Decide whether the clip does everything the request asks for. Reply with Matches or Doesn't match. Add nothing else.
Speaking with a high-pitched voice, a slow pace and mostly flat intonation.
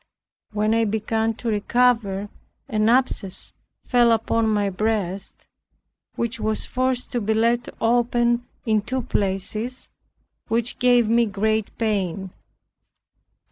Matches